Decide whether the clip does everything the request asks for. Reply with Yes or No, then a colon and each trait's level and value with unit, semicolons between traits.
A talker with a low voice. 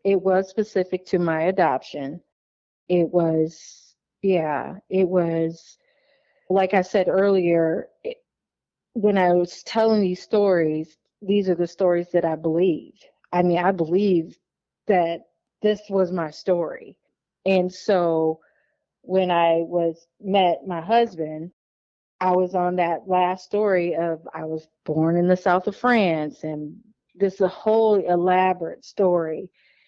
No: medium, 180 Hz